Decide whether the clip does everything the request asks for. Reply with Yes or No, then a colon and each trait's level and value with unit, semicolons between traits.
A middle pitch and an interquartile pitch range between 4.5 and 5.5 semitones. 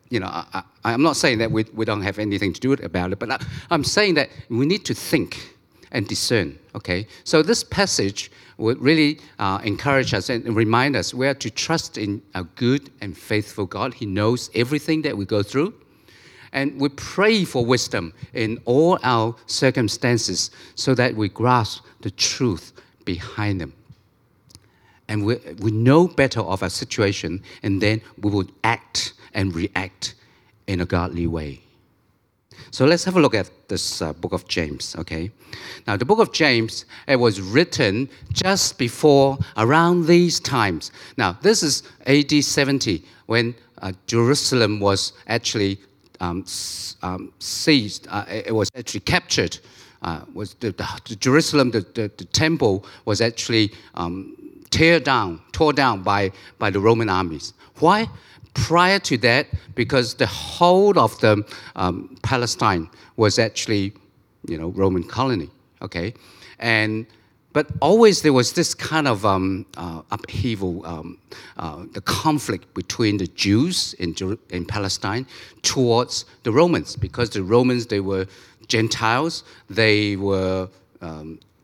No: low, 115 Hz; average, 5.1 semitones